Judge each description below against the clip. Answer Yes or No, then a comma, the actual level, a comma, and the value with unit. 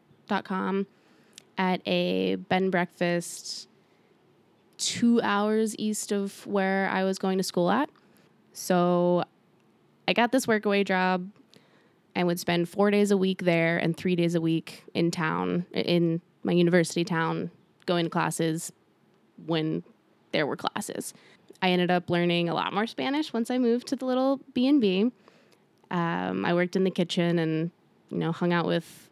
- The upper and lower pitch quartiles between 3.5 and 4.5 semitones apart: No, average, 3.0 semitones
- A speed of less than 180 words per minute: Yes, average, 155 wpm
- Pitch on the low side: No, medium, 180 Hz